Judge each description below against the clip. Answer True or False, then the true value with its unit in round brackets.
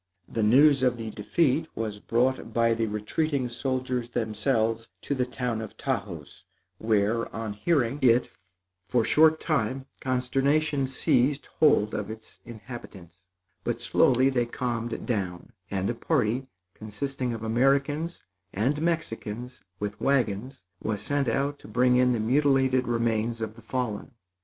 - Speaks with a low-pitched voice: True (120 Hz)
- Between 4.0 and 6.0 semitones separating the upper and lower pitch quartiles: False (3.4 semitones)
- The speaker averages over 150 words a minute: False (140 wpm)